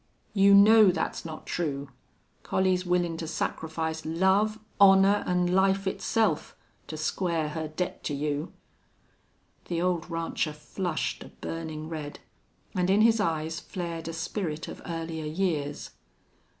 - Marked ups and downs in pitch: No, average, 3.2 semitones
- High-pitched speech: No, medium, 170 Hz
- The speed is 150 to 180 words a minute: No, slow, 135 wpm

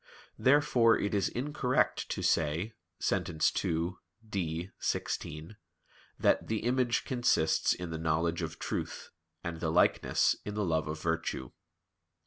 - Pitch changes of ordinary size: No, wide, 6.1 semitones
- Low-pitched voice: Yes, very low, 85 Hz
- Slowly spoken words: Yes, slow, 130 wpm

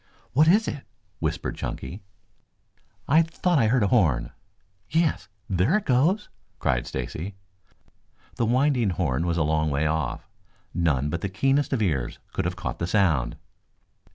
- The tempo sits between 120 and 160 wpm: Yes, average, 155 wpm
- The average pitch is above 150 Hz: No, low, 100 Hz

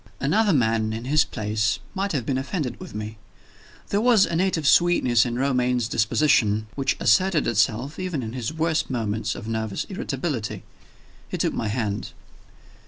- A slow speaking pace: No, average, 160 wpm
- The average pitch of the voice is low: Yes, low, 125 Hz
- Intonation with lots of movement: Yes, wide, 6.3 semitones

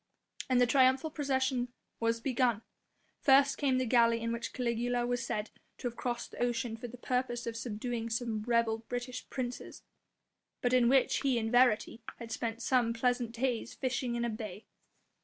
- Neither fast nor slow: Yes, average, 175 wpm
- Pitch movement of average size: No, narrow, 1.7 semitones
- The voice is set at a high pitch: Yes, high, 240 Hz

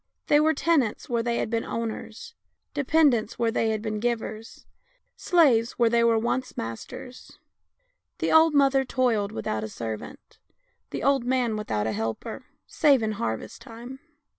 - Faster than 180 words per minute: No, average, 155 wpm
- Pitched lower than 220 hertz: No, high, 235 Hz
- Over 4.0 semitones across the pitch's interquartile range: No, average, 3.7 semitones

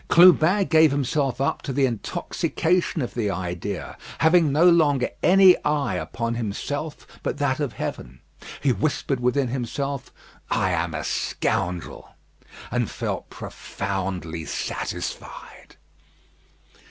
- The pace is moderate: No, slow, 115 wpm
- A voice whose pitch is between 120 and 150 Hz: Yes, low, 135 Hz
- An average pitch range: No, wide, 7.3 semitones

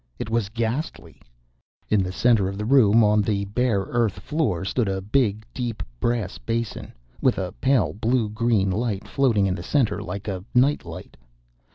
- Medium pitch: No, low, 110 Hz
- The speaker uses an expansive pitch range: No, average, 3.6 semitones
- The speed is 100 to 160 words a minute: No, average, 175 wpm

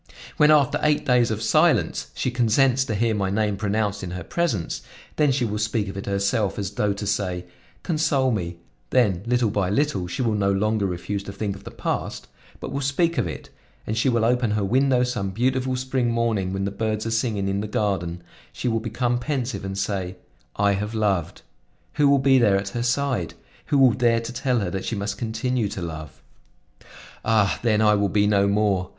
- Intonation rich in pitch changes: No, average, 3.8 semitones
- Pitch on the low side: Yes, low, 110 Hz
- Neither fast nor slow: No, fast, 210 wpm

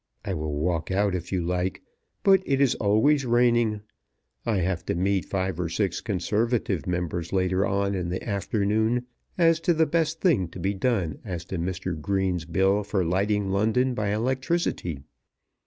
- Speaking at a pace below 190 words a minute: Yes, average, 170 wpm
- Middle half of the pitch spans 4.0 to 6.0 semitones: Yes, average, 4.6 semitones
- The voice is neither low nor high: No, low, 100 Hz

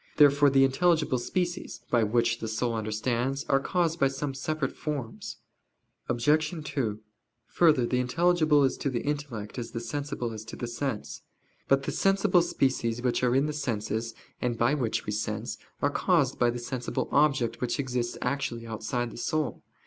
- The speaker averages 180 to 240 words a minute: No, average, 170 wpm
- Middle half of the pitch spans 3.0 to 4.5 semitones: Yes, average, 3.9 semitones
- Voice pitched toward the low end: Yes, low, 130 Hz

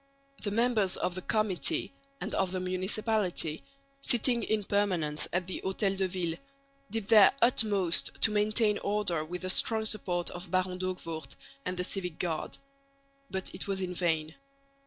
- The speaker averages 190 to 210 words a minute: No, average, 155 wpm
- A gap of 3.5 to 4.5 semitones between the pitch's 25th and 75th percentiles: No, average, 2.9 semitones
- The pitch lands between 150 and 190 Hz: Yes, medium, 185 Hz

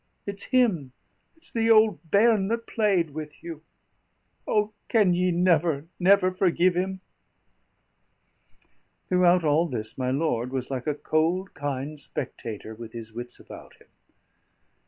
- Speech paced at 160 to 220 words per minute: No, slow, 135 wpm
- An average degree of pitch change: No, wide, 5.8 semitones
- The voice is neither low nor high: Yes, medium, 170 Hz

